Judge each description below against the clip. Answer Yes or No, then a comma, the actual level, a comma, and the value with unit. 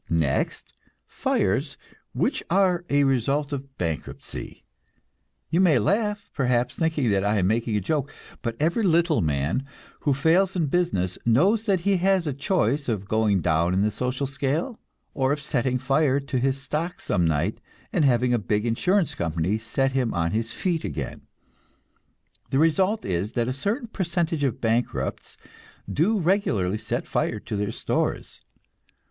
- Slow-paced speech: No, average, 160 wpm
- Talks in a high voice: No, low, 135 Hz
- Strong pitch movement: Yes, wide, 7.7 semitones